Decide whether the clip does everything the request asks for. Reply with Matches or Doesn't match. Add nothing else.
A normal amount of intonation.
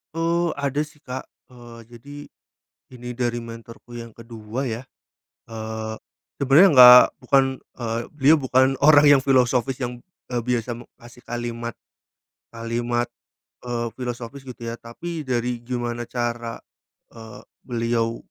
Doesn't match